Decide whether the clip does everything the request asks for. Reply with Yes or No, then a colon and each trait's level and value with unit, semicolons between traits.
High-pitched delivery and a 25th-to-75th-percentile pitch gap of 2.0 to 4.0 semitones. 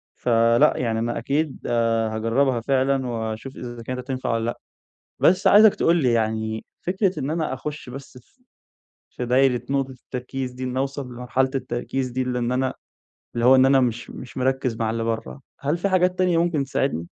No: low, 130 Hz; average, 2.8 semitones